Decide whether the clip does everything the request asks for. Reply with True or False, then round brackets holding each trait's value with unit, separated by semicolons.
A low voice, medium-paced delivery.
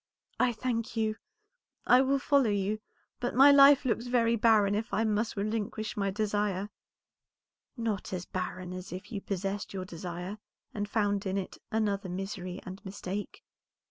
False (205 Hz; 155 wpm)